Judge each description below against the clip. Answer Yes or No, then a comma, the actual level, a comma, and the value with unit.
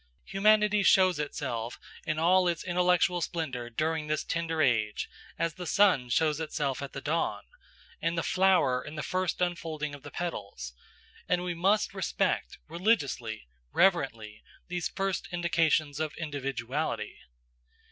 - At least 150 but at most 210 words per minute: No, slow, 135 wpm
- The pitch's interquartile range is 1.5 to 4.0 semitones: No, average, 4.4 semitones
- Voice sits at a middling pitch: Yes, medium, 160 Hz